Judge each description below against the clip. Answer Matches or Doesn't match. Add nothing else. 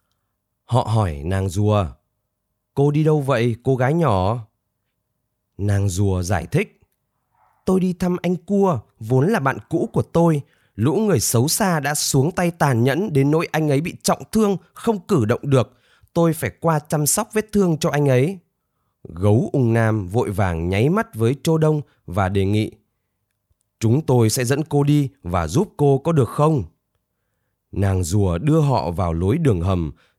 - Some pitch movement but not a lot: Doesn't match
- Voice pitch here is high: Doesn't match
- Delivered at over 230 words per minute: Doesn't match